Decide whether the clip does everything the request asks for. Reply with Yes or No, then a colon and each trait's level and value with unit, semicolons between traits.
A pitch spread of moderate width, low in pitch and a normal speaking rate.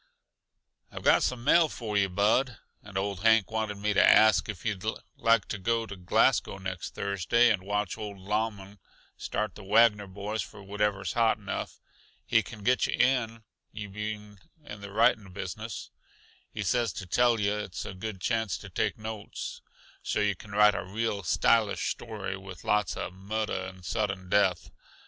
No: narrow, 2.3 semitones; low, 105 Hz; average, 180 wpm